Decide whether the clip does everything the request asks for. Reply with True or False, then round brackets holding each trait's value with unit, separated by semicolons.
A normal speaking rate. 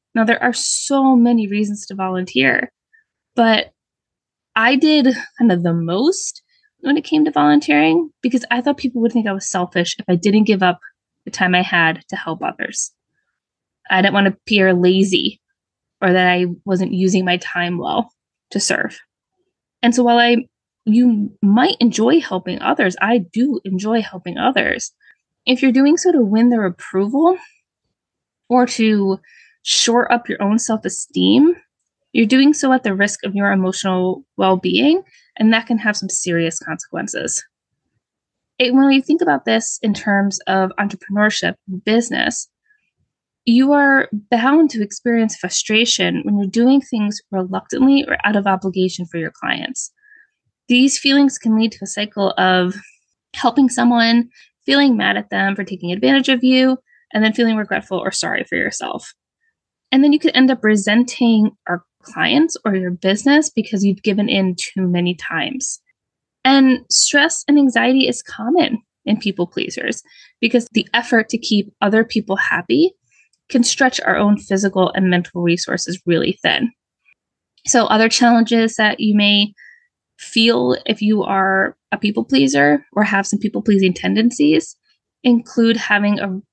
True (155 wpm)